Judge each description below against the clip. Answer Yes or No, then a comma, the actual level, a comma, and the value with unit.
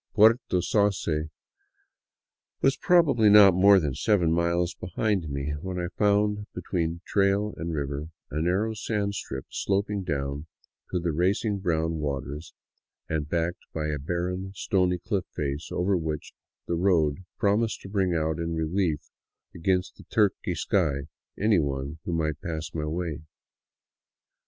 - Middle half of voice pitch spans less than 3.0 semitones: No, average, 4.2 semitones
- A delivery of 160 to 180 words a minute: No, average, 145 wpm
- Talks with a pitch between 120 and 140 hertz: No, very low, 90 Hz